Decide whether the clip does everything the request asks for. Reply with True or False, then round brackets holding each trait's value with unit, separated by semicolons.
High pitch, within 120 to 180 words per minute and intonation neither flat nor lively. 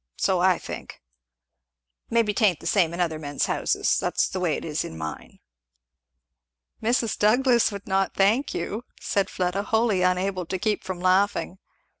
True (195 Hz; 160 wpm; 3.0 semitones)